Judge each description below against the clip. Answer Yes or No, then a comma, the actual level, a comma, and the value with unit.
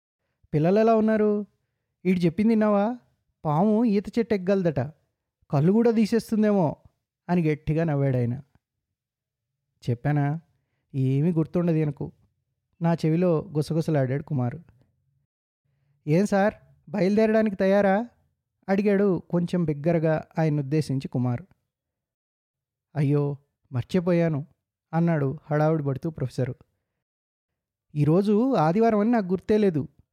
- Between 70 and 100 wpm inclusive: Yes, average, 90 wpm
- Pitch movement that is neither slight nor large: No, wide, 6.3 semitones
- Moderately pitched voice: Yes, medium, 155 Hz